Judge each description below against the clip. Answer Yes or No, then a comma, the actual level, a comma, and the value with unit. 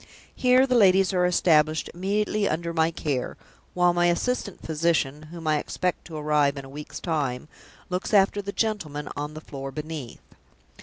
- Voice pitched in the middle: Yes, medium, 165 Hz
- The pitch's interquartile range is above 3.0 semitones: Yes, average, 4.1 semitones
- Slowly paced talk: No, average, 165 wpm